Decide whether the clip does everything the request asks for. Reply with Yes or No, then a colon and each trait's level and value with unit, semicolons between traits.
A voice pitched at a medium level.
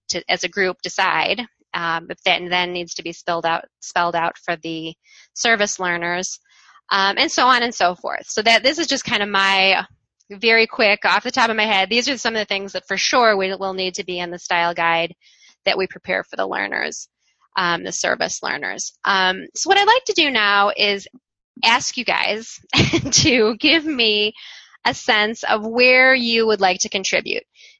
No: high, 200 Hz